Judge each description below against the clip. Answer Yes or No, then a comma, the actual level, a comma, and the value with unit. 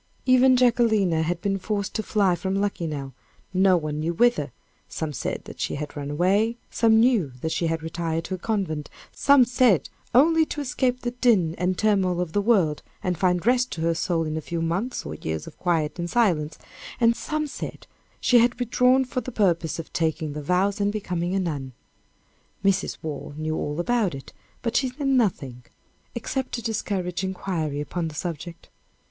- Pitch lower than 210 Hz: Yes, medium, 185 Hz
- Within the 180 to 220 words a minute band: Yes, average, 190 wpm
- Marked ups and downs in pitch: Yes, wide, 6.4 semitones